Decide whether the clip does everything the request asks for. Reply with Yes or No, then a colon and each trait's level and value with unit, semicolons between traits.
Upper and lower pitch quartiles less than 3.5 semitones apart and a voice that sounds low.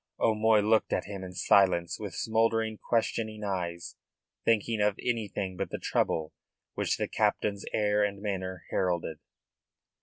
Yes: average, 2.8 semitones; low, 105 Hz